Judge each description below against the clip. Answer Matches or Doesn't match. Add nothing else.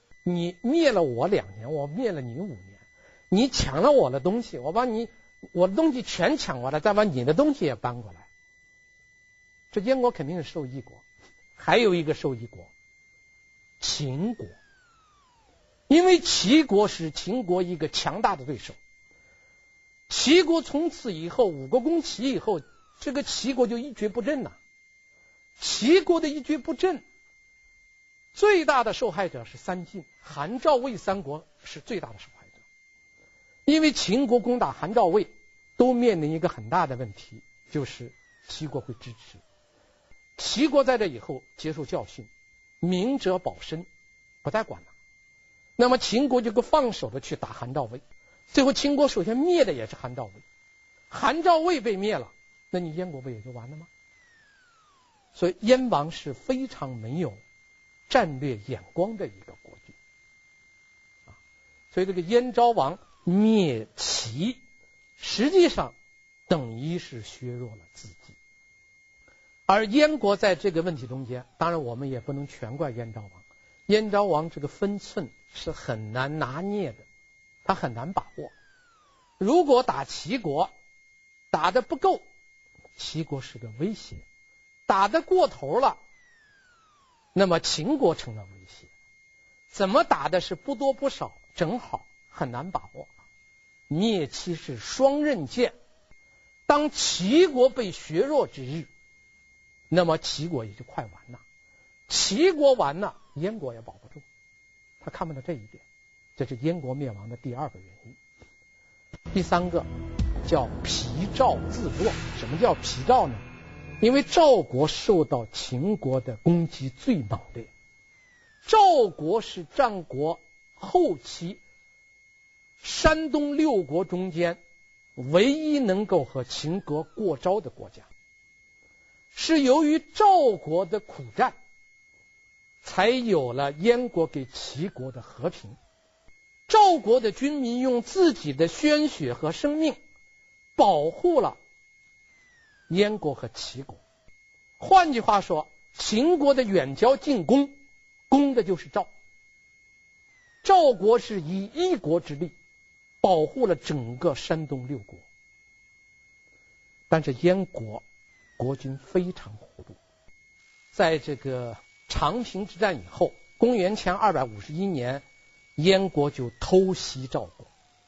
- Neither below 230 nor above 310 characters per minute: Doesn't match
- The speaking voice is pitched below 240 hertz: Matches